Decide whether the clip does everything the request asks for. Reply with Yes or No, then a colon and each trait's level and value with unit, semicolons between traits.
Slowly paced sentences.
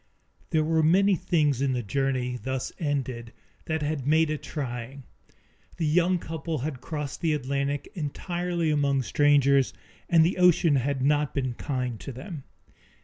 No: average, 150 wpm